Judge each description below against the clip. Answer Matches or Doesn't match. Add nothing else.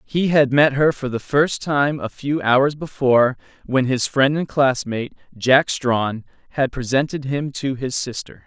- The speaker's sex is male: Matches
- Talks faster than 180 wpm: Doesn't match